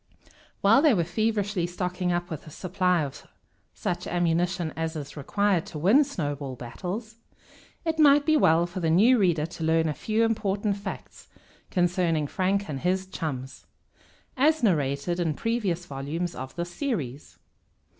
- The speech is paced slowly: No, average, 155 wpm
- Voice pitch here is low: No, medium, 175 Hz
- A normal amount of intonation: Yes, average, 4.3 semitones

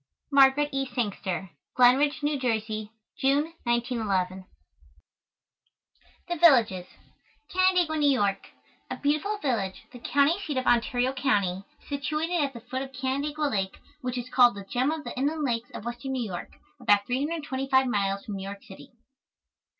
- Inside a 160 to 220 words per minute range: No, average, 150 wpm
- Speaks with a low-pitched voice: No, very high, 255 Hz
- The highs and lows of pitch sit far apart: No, average, 5.0 semitones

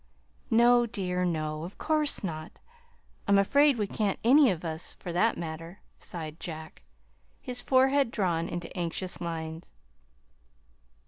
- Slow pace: Yes, slow, 130 wpm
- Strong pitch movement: Yes, wide, 6.2 semitones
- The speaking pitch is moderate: Yes, medium, 180 Hz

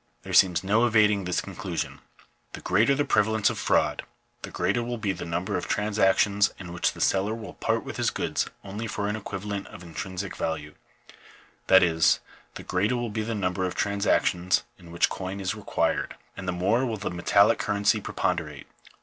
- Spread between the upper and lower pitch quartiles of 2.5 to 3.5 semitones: Yes, average, 2.8 semitones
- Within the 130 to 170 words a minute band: No, average, 190 wpm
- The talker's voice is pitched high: No, low, 100 Hz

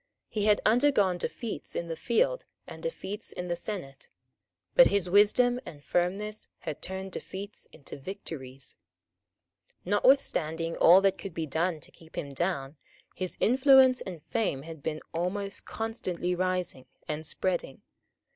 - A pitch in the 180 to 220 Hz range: Yes, medium, 185 Hz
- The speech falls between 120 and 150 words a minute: Yes, average, 140 wpm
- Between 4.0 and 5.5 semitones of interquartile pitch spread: Yes, average, 4.5 semitones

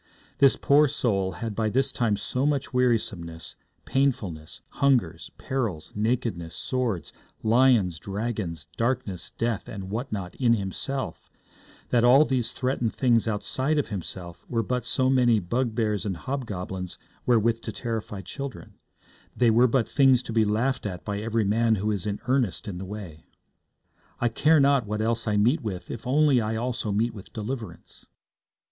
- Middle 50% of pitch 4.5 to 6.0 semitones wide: No, average, 4.0 semitones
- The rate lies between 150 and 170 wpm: Yes, average, 160 wpm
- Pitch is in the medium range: No, low, 115 Hz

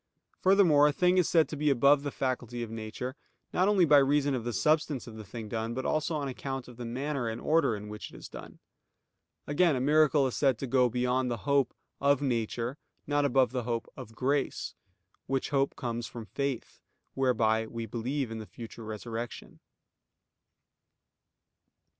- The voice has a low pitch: Yes, low, 130 Hz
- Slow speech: No, average, 185 wpm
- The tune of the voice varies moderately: Yes, average, 3.7 semitones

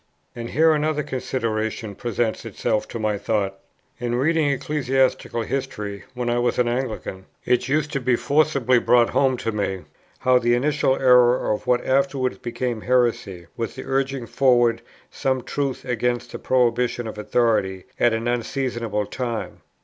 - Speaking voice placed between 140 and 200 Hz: No, low, 120 Hz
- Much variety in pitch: No, narrow, 2.5 semitones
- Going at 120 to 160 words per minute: Yes, average, 155 wpm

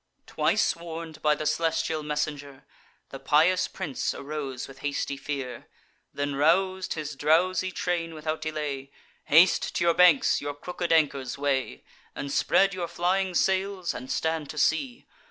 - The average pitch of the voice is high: No, medium, 155 Hz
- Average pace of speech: Yes, average, 145 wpm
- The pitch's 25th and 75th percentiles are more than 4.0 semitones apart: No, average, 3.3 semitones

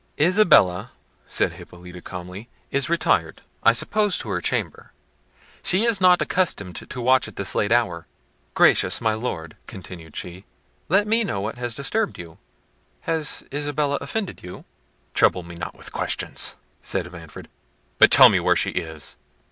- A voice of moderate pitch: No, low, 110 Hz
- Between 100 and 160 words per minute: Yes, average, 155 wpm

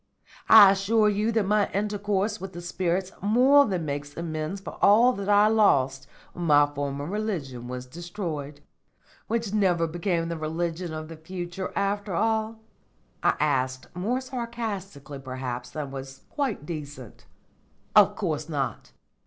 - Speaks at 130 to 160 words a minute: Yes, average, 145 wpm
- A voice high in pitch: No, medium, 175 Hz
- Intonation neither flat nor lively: No, wide, 6.2 semitones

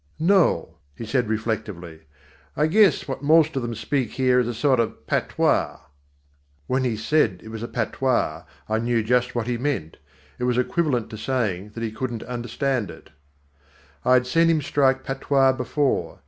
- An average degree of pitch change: Yes, average, 3.5 semitones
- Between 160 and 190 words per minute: Yes, average, 175 wpm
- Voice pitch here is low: Yes, low, 125 Hz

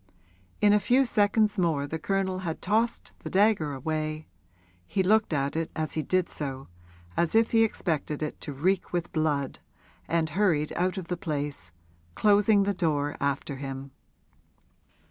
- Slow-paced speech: No, average, 160 wpm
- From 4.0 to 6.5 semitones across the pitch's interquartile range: Yes, average, 5.3 semitones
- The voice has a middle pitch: Yes, medium, 165 Hz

